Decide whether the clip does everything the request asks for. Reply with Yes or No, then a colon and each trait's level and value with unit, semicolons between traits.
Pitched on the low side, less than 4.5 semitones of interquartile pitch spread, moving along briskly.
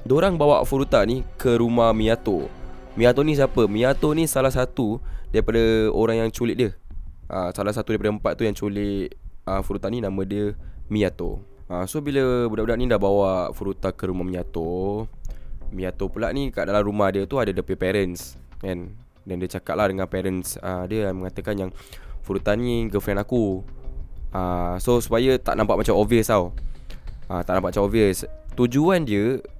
Yes: low, 100 Hz; average, 4.1 semitones; fast, 160 wpm